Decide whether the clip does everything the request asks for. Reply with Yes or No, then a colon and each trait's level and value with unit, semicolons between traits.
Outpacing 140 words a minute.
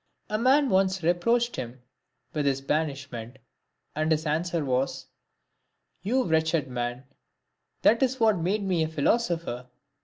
No: slow, 135 wpm